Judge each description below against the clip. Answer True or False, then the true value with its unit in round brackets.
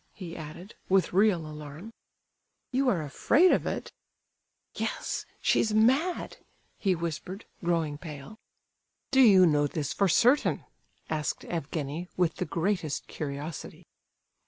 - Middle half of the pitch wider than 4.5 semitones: True (5.4 semitones)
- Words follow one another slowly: True (115 wpm)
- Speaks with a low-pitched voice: False (175 Hz)